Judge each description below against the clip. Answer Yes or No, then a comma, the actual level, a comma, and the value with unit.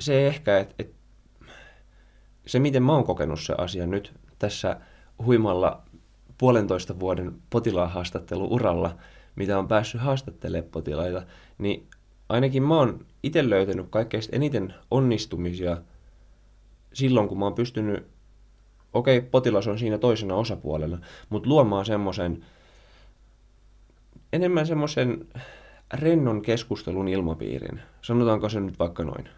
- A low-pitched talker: Yes, low, 105 Hz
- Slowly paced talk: No, average, 115 wpm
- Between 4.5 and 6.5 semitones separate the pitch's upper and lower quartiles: Yes, average, 5.1 semitones